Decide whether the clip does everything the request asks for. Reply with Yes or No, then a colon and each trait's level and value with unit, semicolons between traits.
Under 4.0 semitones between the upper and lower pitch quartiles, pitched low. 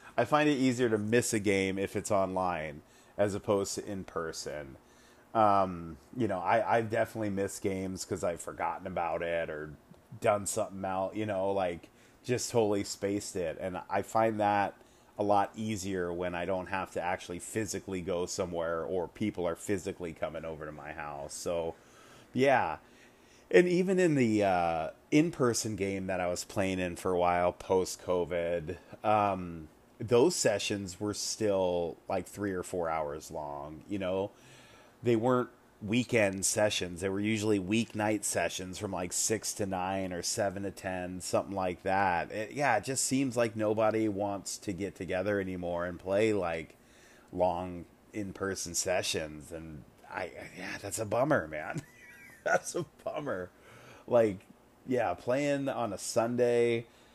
Yes: average, 3.4 semitones; low, 100 Hz